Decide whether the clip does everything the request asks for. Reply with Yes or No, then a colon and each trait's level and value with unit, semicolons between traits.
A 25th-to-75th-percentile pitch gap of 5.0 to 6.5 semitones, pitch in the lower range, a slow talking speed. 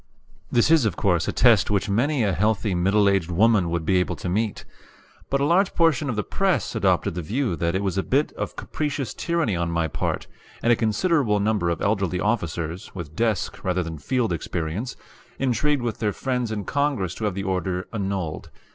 No: average, 5.3 semitones; low, 105 Hz; average, 200 wpm